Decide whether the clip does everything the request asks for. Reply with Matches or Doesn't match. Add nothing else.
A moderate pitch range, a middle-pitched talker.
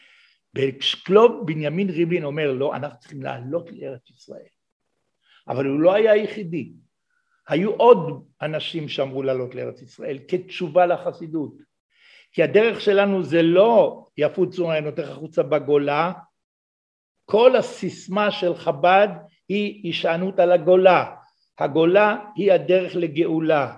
Matches